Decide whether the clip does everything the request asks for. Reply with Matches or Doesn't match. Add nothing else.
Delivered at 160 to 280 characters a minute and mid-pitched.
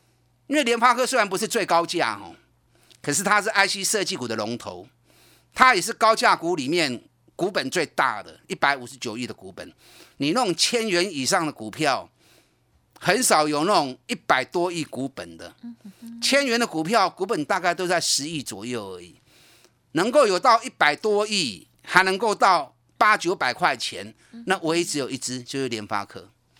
Matches